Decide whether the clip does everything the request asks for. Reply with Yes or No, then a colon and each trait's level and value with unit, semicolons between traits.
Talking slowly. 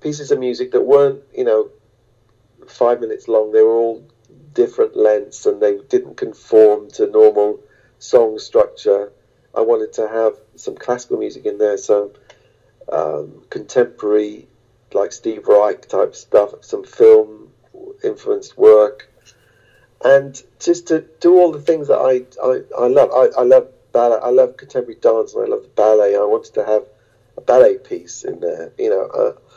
No: average, 165 wpm